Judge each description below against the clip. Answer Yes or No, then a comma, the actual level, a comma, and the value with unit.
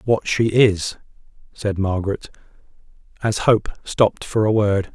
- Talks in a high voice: No, low, 105 Hz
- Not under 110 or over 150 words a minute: Yes, slow, 135 wpm